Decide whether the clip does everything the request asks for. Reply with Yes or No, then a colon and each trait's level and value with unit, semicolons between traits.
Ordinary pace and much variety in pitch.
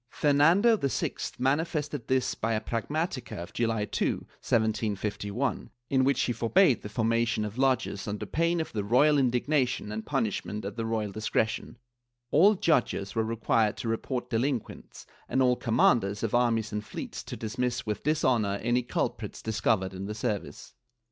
No: average, 160 wpm; average, 3.8 semitones